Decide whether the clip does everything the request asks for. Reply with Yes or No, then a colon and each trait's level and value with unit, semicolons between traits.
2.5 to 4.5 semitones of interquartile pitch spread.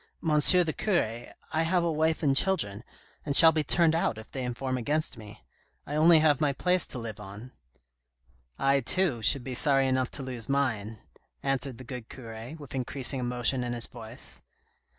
No: average, 4.9 semitones